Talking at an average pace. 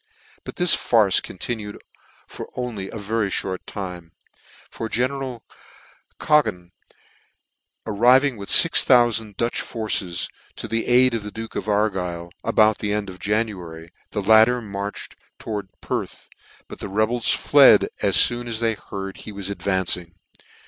Yes: average, 150 wpm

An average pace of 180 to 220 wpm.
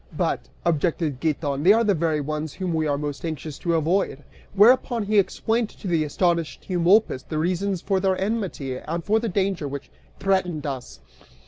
No: average, 170 wpm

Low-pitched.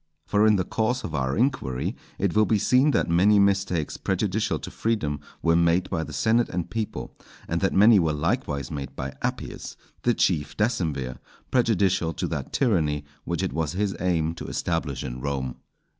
Yes: very low, 90 Hz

